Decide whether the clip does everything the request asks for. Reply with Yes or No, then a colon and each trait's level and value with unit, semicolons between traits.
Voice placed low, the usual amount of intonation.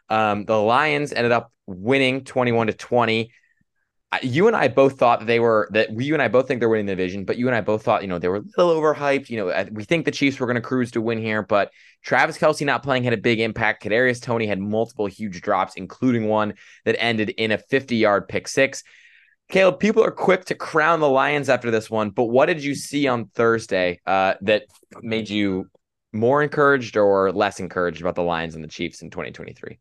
Yes: low, 115 Hz; average, 4.3 semitones